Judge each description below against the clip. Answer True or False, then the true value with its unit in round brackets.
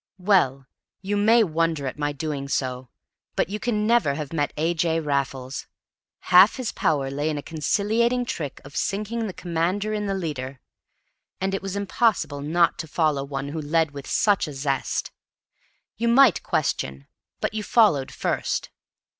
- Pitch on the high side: False (165 Hz)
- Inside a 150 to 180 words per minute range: True (165 wpm)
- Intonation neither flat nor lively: False (6.3 semitones)